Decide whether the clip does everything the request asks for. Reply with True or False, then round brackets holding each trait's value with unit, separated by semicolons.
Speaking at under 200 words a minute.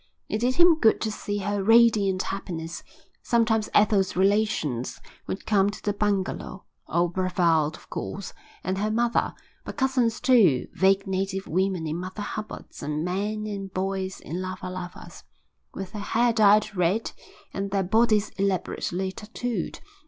True (150 wpm)